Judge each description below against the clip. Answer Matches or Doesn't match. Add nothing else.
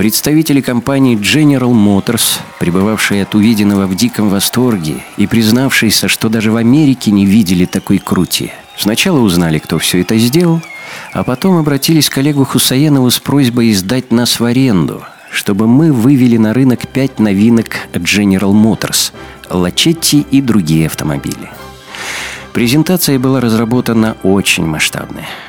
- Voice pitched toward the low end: Matches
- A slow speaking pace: Doesn't match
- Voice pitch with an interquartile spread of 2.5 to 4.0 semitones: Doesn't match